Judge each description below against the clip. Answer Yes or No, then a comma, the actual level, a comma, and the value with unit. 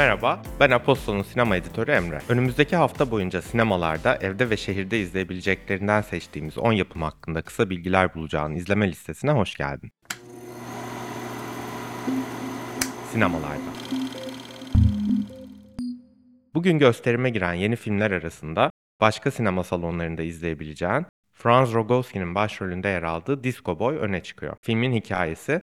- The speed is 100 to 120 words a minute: Yes, average, 110 wpm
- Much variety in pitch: Yes, wide, 6.5 semitones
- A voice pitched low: Yes, low, 105 Hz